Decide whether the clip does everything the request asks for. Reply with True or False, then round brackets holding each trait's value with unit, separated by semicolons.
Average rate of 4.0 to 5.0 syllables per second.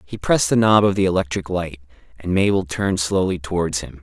False (5.9 syllables/s)